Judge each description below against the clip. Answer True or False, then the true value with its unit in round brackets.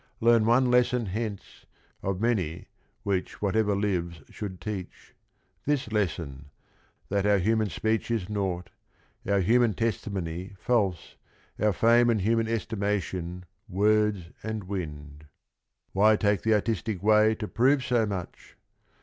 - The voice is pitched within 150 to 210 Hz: False (105 Hz)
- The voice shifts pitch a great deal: False (3.3 semitones)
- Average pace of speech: False (125 wpm)